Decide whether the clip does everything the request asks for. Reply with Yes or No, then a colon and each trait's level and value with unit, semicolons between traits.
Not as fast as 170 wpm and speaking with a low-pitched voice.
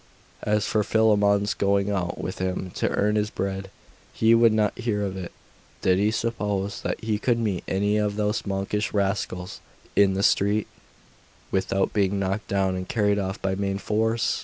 No: average, 175 wpm; low, 100 Hz